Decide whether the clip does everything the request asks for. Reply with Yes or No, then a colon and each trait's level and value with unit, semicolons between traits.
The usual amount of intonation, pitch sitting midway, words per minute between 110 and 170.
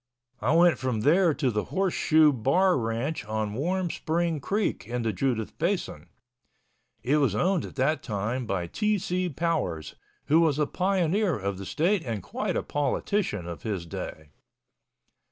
No: wide, 8.2 semitones; medium, 145 Hz; average, 165 wpm